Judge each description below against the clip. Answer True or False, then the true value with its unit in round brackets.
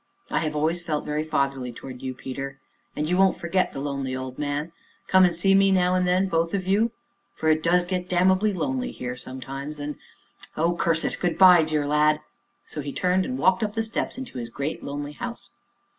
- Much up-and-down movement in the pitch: False (4.5 semitones)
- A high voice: False (165 Hz)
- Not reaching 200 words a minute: False (205 wpm)